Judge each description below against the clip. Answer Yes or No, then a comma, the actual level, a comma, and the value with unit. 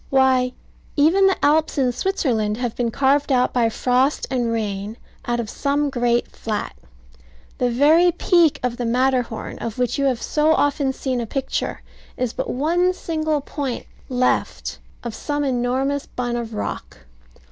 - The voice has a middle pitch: No, very high, 255 Hz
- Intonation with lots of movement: No, average, 3.2 semitones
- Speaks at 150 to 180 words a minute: Yes, average, 160 wpm